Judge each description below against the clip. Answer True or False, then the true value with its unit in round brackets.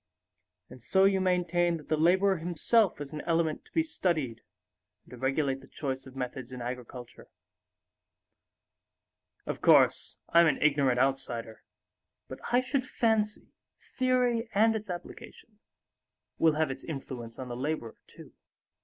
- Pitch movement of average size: False (6.7 semitones)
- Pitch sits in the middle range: True (155 Hz)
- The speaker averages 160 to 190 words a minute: False (145 wpm)